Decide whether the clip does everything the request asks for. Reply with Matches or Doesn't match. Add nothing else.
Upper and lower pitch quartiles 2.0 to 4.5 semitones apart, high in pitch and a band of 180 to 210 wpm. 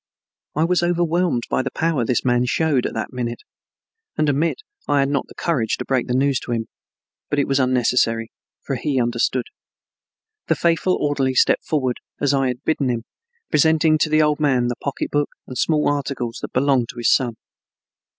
Doesn't match